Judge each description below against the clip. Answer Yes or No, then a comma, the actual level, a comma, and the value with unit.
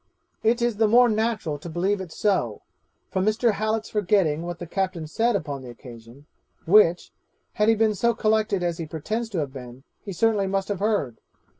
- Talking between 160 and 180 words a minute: No, average, 195 wpm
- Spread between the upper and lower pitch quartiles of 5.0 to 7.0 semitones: Yes, average, 5.3 semitones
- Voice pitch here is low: No, high, 195 Hz